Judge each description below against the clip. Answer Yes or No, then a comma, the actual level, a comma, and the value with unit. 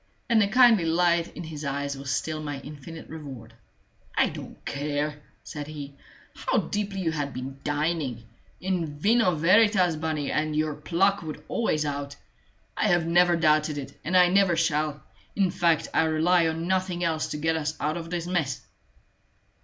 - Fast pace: No, average, 170 wpm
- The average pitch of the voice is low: No, medium, 160 Hz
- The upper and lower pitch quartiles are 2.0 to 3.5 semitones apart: Yes, average, 3.0 semitones